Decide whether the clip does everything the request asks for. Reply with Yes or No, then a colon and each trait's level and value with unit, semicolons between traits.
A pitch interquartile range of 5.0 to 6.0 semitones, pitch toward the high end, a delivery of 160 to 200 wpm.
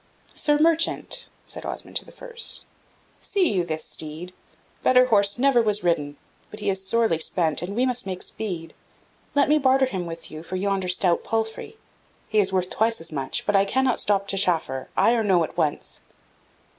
Yes: wide, 5.6 semitones; high, 200 Hz; average, 190 wpm